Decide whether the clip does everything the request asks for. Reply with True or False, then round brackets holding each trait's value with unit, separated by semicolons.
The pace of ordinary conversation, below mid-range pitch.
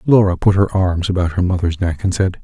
False (245 wpm; 90 Hz)